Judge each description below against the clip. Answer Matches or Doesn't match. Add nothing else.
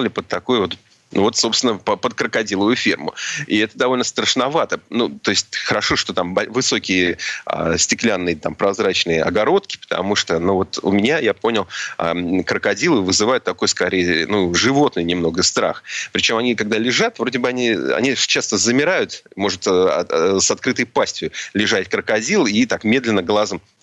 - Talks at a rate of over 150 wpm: Matches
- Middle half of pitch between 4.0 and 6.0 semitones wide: Doesn't match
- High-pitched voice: Doesn't match